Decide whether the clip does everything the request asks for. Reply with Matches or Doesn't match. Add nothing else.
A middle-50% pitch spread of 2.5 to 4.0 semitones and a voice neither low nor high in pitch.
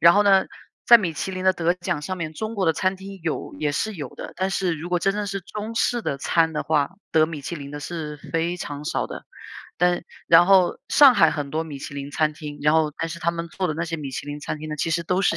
Matches